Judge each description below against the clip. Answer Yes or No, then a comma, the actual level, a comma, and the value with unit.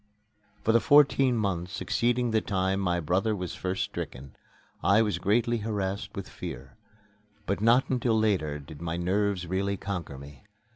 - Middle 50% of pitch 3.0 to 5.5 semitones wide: Yes, average, 4.2 semitones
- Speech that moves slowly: No, average, 155 wpm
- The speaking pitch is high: No, low, 100 Hz